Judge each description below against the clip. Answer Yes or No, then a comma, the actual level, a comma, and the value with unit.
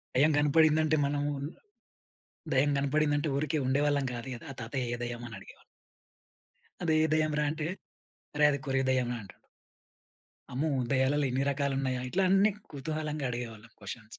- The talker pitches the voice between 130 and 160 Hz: Yes, medium, 140 Hz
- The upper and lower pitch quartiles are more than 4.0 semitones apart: No, average, 3.1 semitones